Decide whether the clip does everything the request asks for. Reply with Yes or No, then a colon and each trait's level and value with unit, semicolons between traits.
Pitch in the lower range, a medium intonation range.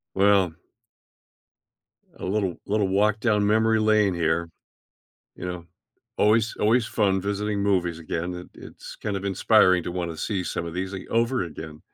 Yes: low, 100 Hz; average, 3.3 semitones